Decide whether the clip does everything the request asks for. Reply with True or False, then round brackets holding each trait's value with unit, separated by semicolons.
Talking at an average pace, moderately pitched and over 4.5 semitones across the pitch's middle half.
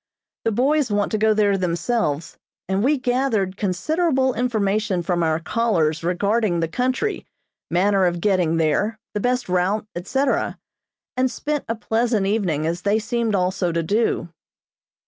False (145 wpm; 205 Hz; 5.1 semitones)